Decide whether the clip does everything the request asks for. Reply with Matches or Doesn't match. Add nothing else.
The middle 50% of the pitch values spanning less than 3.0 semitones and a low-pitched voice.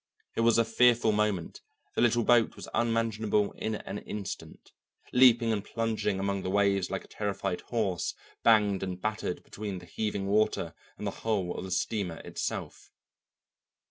Matches